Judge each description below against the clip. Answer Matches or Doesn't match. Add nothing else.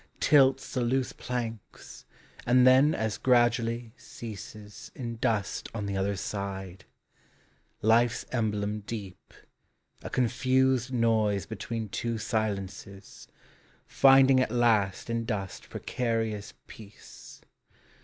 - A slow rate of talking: Matches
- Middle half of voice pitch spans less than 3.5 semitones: Matches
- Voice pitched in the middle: Doesn't match